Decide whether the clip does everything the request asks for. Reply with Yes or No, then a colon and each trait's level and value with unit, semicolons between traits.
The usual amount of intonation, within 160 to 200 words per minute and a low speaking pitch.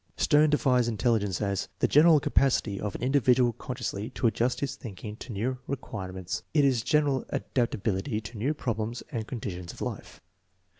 Yes: average, 4.2 semitones; average, 180 wpm; low, 120 Hz